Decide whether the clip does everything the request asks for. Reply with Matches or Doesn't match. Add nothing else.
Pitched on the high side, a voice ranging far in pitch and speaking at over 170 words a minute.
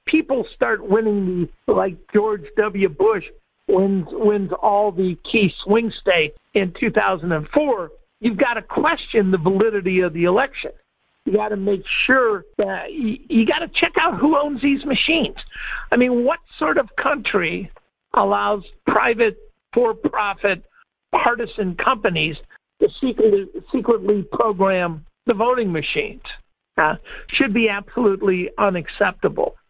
Doesn't match